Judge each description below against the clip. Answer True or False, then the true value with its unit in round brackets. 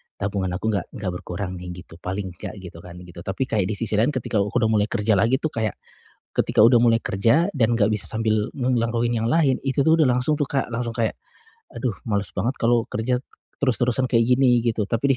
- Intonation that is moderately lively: True (3.6 semitones)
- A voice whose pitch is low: True (115 Hz)